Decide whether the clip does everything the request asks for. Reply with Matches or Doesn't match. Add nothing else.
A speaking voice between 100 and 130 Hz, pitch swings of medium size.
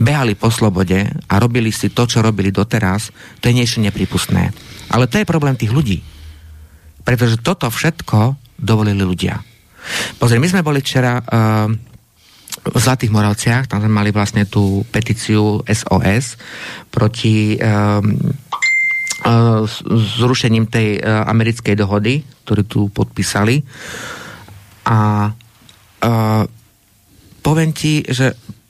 Matches